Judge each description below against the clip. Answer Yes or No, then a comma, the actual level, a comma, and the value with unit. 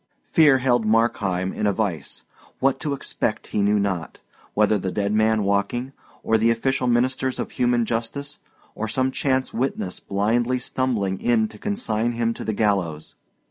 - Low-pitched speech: Yes, low, 115 Hz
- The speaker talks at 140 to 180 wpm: Yes, average, 165 wpm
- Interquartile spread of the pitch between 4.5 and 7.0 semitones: No, average, 3.9 semitones